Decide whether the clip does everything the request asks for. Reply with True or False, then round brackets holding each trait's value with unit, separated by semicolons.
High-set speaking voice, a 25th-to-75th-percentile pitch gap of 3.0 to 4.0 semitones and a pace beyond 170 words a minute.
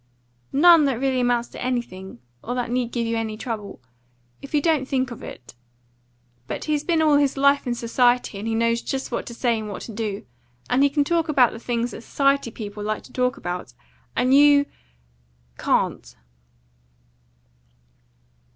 True (245 Hz; 3.6 semitones; 180 wpm)